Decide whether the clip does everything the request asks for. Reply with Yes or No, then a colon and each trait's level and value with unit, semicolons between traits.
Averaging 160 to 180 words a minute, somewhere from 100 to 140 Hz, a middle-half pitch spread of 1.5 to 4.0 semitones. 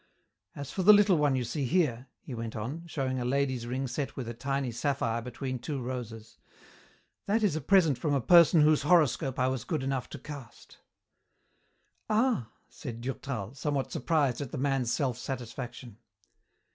Yes: average, 170 wpm; low, 135 Hz; average, 3.5 semitones